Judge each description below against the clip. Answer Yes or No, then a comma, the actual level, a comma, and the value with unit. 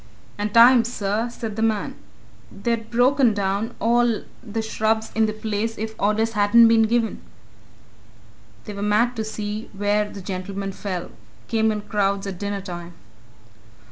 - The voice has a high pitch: Yes, high, 215 Hz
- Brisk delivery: No, average, 150 wpm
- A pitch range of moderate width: No, narrow, 1.9 semitones